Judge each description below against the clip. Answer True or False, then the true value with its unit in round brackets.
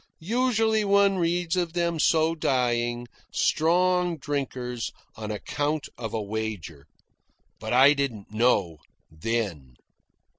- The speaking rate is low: True (110 wpm)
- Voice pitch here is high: False (135 Hz)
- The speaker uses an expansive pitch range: True (7.7 semitones)